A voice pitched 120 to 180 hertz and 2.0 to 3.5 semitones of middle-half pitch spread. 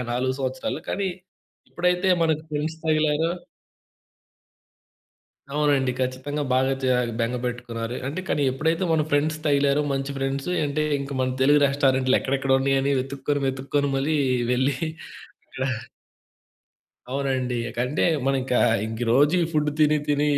Yes: medium, 140 Hz; narrow, 2.4 semitones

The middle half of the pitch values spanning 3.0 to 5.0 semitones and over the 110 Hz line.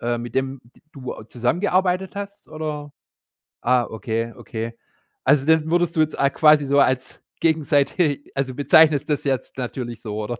Yes: average, 4.5 semitones; medium, 140 Hz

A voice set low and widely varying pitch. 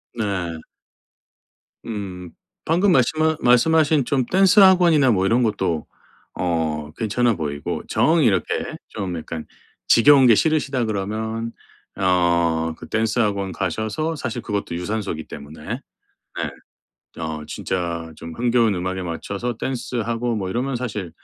Yes: low, 110 Hz; wide, 6.0 semitones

